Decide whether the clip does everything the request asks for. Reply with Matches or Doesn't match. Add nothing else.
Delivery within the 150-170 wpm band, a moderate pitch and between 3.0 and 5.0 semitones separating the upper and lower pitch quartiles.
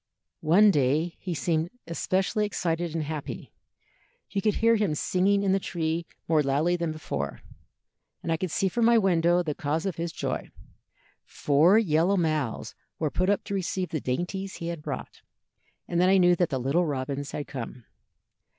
Doesn't match